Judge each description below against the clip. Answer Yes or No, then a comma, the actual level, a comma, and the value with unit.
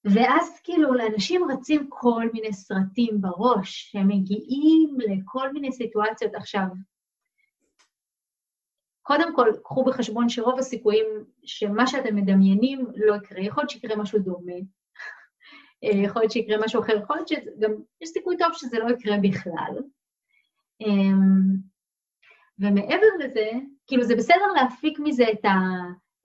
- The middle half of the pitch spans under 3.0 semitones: No, average, 5.3 semitones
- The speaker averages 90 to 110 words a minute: No, average, 125 wpm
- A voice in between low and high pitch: No, high, 230 Hz